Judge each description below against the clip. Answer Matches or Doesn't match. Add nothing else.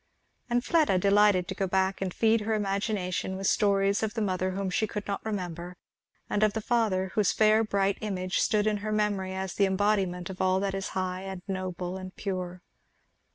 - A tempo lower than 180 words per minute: Doesn't match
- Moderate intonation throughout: Doesn't match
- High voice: Matches